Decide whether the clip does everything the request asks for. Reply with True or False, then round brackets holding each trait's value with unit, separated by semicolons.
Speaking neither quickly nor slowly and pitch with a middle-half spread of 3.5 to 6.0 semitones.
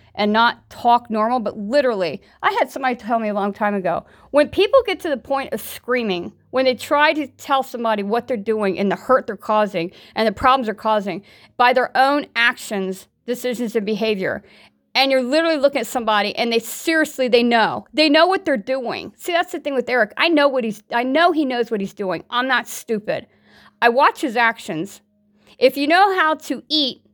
False (210 wpm; 4.6 semitones)